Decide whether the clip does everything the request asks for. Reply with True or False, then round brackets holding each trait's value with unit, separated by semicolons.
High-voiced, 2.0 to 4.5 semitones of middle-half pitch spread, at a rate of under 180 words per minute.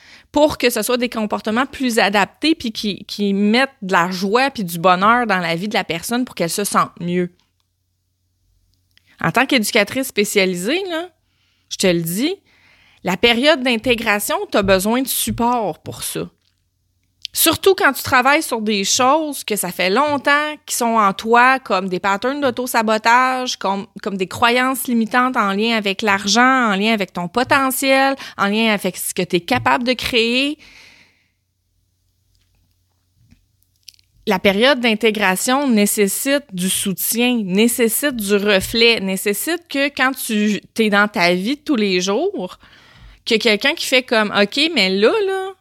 False (220 Hz; 5.4 semitones; 160 wpm)